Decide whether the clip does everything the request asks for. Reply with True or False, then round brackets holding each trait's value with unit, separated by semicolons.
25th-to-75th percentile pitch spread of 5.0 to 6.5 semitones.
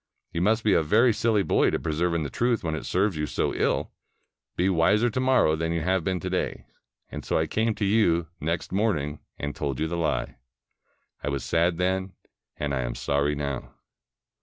True (5.3 semitones)